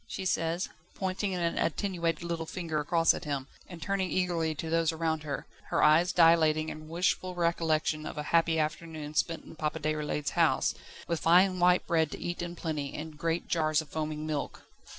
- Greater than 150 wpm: Yes, average, 185 wpm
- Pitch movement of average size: No, narrow, 1.9 semitones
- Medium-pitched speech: Yes, medium, 165 Hz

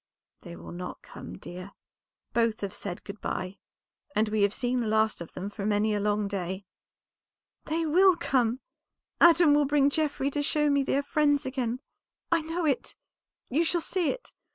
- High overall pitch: Yes, very high, 255 Hz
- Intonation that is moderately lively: No, wide, 6.5 semitones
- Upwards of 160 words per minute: Yes, average, 180 wpm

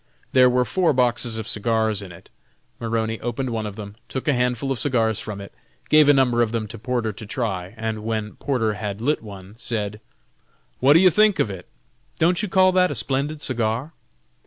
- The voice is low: Yes, low, 115 Hz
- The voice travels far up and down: No, average, 3.8 semitones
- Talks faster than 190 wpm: Yes, fast, 205 wpm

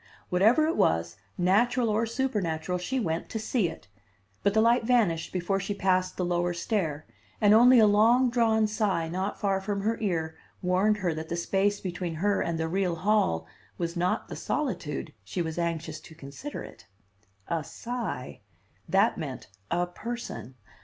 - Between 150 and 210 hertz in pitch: Yes, high, 190 Hz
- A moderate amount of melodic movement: Yes, average, 4.7 semitones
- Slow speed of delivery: No, average, 170 wpm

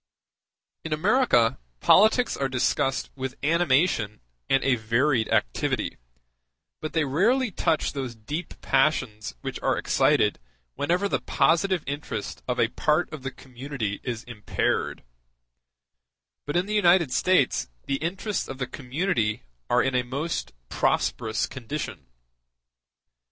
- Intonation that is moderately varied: No, wide, 5.7 semitones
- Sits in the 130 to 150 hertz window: Yes, low, 135 Hz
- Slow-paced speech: Yes, slow, 125 wpm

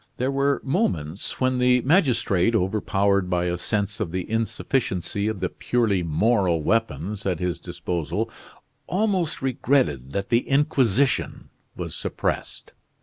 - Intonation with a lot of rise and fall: Yes, wide, 6.1 semitones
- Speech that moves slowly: Yes, slow, 130 wpm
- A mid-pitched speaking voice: No, low, 105 Hz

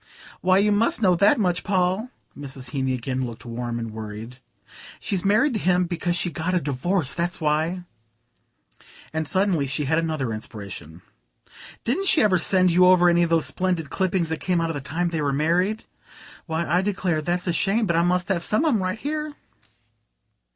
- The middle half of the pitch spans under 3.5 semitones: No, average, 4.5 semitones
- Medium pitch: Yes, medium, 175 Hz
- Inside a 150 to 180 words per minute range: No, average, 190 wpm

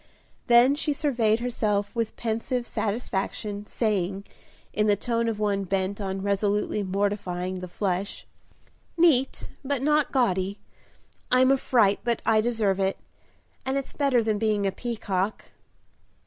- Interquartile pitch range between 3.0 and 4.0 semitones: Yes, average, 3.4 semitones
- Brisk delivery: No, slow, 135 wpm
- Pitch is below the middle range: No, high, 215 Hz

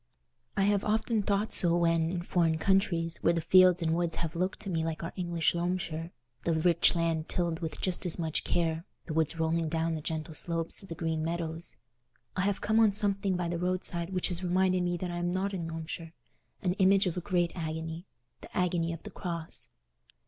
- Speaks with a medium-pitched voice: Yes, medium, 170 Hz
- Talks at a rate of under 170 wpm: No, average, 200 wpm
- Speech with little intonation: Yes, narrow, 2.1 semitones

